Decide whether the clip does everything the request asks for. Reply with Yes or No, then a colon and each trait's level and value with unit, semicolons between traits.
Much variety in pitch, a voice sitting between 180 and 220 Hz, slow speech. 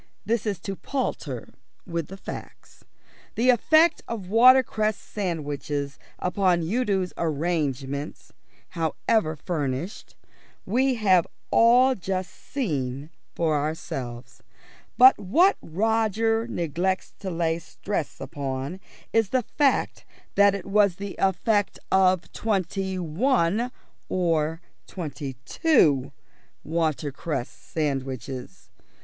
Yes: wide, 6.0 semitones; medium, 185 Hz; slow, 100 wpm